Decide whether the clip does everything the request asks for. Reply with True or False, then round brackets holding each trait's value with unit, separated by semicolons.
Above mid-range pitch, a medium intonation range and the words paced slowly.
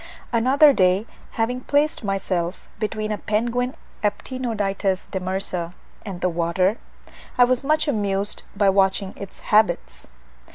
True (205 Hz; 4.3 semitones; 120 wpm)